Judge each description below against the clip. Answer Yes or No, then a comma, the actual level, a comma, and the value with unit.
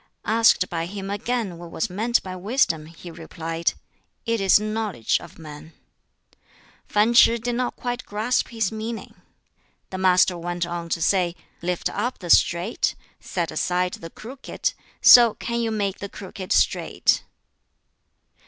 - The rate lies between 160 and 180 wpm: No, average, 145 wpm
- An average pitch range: Yes, average, 4.6 semitones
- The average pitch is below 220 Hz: Yes, high, 190 Hz